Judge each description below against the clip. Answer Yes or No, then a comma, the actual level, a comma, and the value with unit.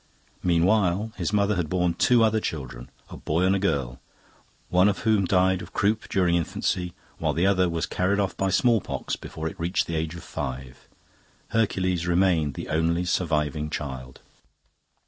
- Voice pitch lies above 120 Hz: No, very low, 90 Hz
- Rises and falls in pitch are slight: No, average, 3.5 semitones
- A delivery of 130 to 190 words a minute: Yes, average, 165 wpm